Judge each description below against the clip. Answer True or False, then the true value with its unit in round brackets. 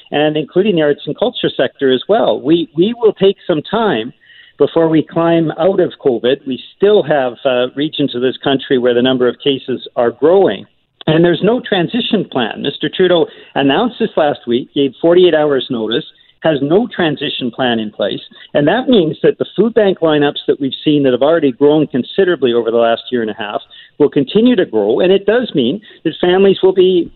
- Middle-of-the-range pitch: True (155 Hz)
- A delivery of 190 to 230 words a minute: True (205 wpm)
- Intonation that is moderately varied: False (6.6 semitones)